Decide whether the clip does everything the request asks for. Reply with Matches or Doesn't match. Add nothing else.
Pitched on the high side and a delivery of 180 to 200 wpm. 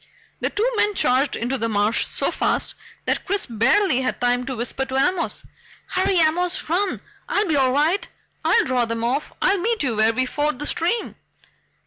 Matches